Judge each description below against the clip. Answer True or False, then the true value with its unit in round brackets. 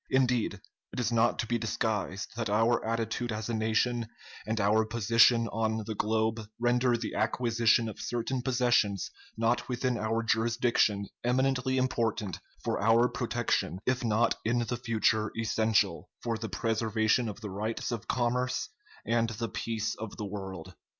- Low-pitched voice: True (115 Hz)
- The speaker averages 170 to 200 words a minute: False (155 wpm)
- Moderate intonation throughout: False (1.6 semitones)